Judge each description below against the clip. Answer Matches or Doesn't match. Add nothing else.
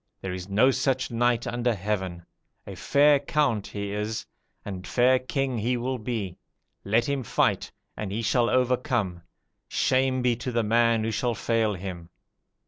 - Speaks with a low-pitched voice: Matches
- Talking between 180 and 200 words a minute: Doesn't match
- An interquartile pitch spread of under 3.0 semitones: Doesn't match